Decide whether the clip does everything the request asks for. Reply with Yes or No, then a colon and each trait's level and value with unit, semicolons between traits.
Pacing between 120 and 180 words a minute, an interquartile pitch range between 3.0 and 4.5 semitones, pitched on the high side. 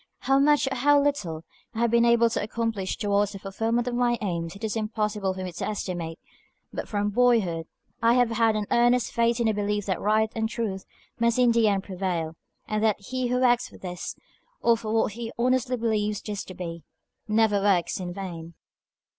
No: fast, 205 wpm; average, 3.4 semitones; high, 215 Hz